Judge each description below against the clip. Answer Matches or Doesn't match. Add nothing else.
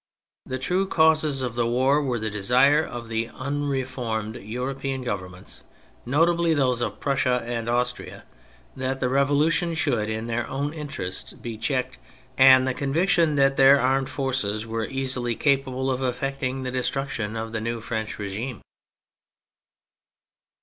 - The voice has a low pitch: Matches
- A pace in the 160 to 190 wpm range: Doesn't match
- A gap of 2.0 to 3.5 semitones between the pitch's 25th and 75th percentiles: Matches